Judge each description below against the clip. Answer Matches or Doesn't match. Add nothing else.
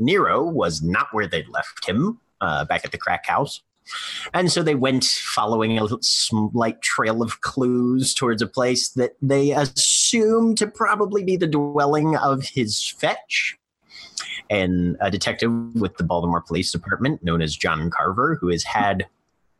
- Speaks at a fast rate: Doesn't match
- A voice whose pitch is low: Matches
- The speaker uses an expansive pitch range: Matches